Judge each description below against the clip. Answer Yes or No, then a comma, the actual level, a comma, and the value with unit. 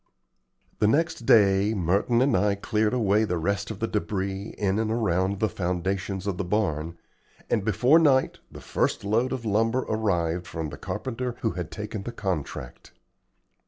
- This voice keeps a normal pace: Yes, average, 165 wpm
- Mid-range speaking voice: No, low, 100 Hz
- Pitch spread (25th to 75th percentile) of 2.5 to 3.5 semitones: Yes, average, 3.2 semitones